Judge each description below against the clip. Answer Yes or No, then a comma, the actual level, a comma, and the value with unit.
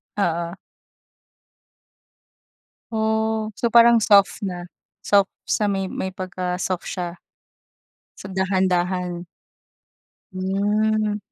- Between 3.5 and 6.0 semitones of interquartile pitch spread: No, average, 2.9 semitones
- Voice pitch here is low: No, high, 195 Hz